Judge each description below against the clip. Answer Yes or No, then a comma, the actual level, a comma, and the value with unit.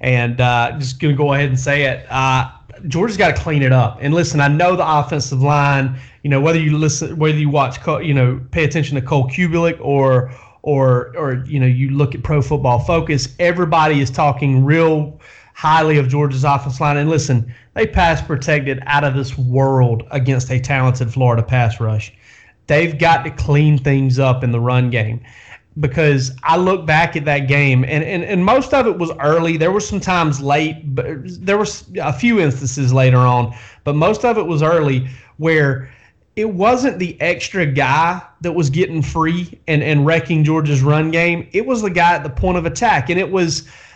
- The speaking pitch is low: No, medium, 145 Hz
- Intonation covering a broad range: No, average, 3.9 semitones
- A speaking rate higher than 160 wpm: Yes, average, 200 wpm